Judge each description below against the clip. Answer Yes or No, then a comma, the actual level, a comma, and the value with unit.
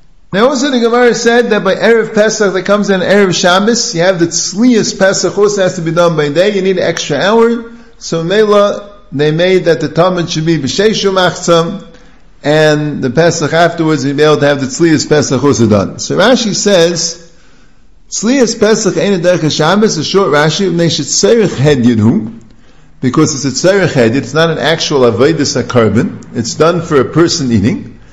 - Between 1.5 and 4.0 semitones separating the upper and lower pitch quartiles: No, average, 5.0 semitones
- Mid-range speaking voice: Yes, medium, 170 Hz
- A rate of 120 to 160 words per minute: No, average, 175 wpm